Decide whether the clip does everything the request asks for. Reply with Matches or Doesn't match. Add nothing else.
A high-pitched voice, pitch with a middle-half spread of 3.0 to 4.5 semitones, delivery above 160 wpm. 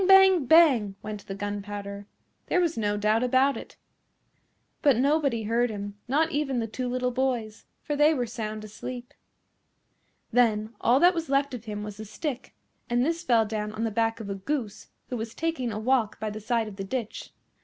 Matches